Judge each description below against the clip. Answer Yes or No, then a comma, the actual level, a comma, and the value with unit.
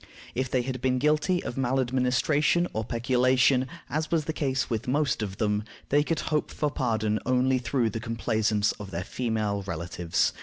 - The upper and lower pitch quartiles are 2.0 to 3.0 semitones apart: No, average, 3.7 semitones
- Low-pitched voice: Yes, low, 125 Hz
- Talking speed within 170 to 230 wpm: Yes, average, 175 wpm